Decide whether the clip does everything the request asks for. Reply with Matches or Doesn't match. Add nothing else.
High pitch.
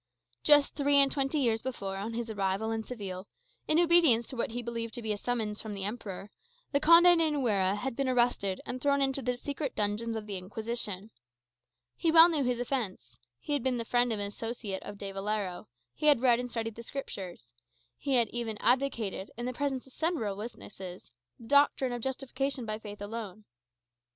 Matches